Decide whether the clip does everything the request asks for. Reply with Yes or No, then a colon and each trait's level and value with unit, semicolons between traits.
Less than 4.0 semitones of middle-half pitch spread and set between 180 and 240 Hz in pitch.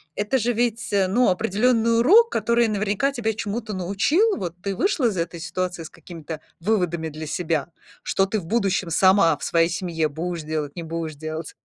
No: average, 5.3 semitones; high, 190 Hz